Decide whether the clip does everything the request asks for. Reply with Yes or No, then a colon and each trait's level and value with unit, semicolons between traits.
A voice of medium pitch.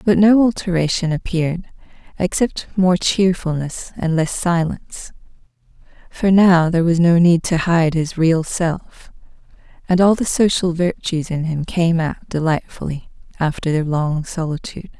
Yes: medium, 170 Hz